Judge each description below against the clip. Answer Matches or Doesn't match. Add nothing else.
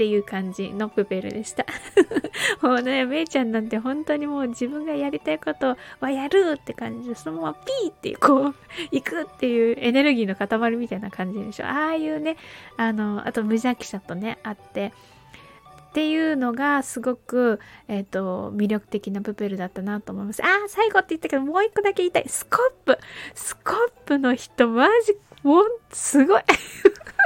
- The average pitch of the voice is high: Matches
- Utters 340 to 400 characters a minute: Matches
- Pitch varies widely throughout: Matches